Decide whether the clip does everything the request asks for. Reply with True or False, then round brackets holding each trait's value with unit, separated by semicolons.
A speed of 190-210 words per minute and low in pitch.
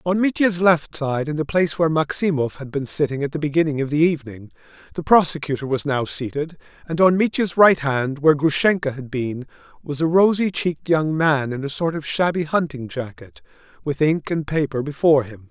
False (195 wpm; 150 Hz)